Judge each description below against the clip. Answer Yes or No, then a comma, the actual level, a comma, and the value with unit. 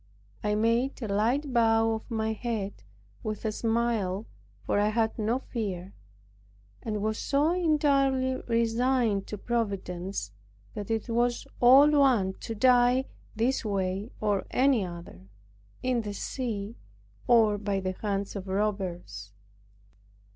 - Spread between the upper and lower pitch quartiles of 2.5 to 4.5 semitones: Yes, average, 3.4 semitones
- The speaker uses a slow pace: Yes, slow, 130 wpm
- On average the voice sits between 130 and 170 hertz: No, high, 220 Hz